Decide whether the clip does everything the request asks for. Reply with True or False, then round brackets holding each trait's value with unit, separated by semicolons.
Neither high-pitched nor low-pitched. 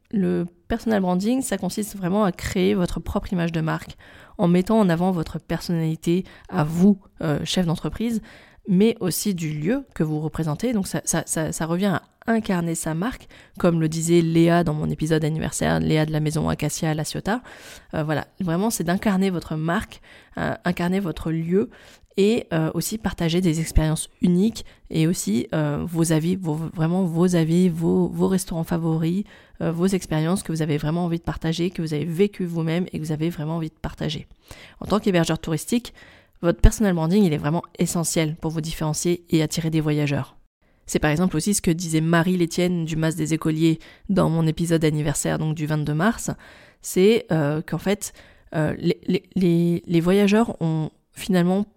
True (170 Hz)